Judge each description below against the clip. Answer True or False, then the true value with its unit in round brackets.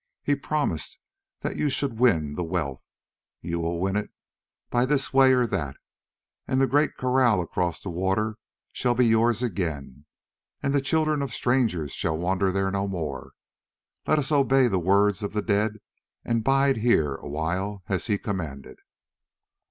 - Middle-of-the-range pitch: False (105 Hz)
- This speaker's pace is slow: False (160 wpm)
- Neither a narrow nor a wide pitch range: False (6.8 semitones)